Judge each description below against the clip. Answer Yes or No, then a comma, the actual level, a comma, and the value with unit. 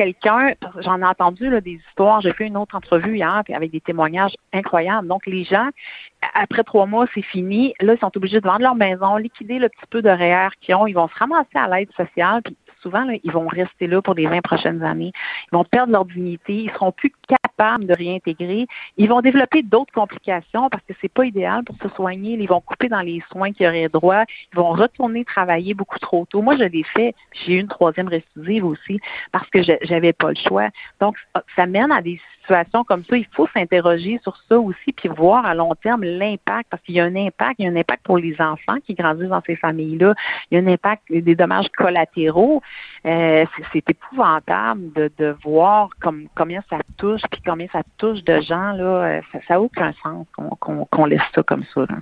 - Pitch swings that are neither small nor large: Yes, average, 4.0 semitones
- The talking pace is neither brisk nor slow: No, fast, 225 wpm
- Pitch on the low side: No, high, 190 Hz